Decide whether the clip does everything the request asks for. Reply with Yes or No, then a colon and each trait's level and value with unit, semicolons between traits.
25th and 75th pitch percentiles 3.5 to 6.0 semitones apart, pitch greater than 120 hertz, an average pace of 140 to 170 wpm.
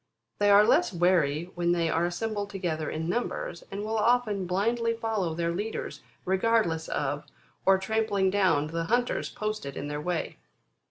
Yes: average, 4.5 semitones; high, 190 Hz; average, 160 wpm